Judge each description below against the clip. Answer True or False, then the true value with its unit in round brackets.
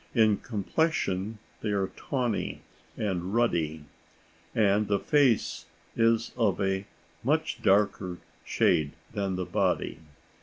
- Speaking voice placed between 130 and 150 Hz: False (100 Hz)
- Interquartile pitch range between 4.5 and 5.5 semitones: False (3.2 semitones)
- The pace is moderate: False (110 wpm)